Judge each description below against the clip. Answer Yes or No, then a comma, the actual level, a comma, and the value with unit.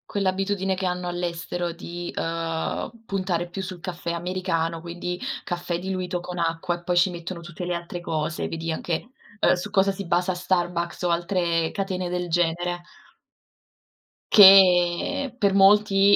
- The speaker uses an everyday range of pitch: No, narrow, 1.7 semitones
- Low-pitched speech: No, medium, 175 Hz